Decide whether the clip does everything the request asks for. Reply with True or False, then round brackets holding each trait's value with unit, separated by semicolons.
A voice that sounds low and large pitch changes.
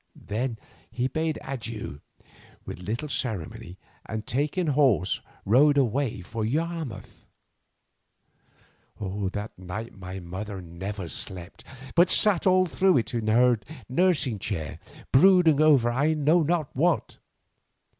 True (120 Hz; 6.8 semitones)